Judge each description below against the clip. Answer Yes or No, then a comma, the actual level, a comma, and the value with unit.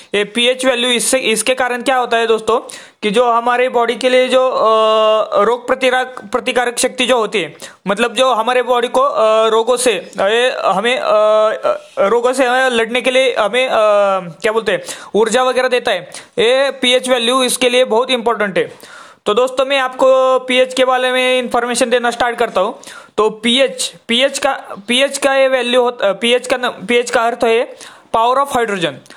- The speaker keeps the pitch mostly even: Yes, narrow, 1.8 semitones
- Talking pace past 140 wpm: Yes, average, 175 wpm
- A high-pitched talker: Yes, very high, 250 Hz